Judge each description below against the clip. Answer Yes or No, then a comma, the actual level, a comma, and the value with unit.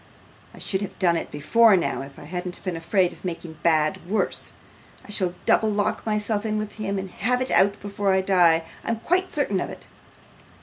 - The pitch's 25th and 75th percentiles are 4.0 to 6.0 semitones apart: No, average, 3.5 semitones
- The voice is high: Yes, high, 195 Hz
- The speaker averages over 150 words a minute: Yes, fast, 205 wpm